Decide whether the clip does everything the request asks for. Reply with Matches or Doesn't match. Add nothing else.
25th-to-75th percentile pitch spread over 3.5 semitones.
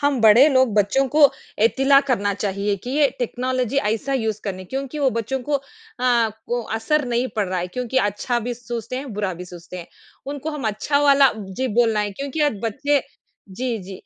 Matches